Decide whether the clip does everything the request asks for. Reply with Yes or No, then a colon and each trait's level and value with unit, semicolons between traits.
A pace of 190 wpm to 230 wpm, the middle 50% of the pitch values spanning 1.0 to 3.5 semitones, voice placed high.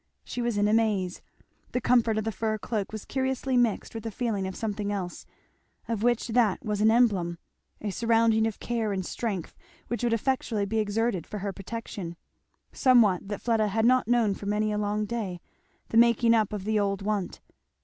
Yes: average, 195 wpm; narrow, 2.4 semitones; high, 215 Hz